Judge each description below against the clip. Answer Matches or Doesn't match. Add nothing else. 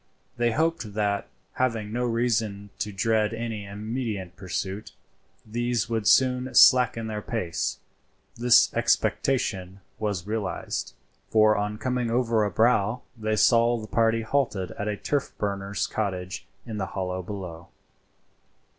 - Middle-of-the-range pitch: Doesn't match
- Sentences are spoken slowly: Matches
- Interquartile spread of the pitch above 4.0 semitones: Doesn't match